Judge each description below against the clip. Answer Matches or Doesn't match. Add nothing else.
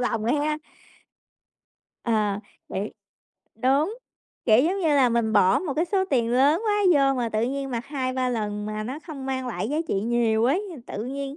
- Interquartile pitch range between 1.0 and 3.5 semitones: Doesn't match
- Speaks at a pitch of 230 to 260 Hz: Matches